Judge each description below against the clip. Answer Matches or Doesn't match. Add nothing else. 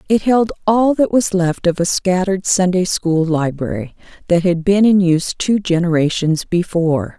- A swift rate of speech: Doesn't match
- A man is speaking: Doesn't match